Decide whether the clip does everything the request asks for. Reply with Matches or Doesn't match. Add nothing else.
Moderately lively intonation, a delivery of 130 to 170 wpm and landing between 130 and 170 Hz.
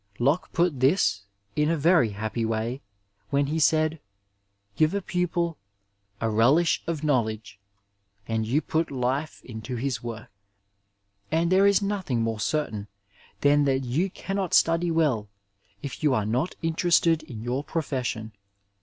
Doesn't match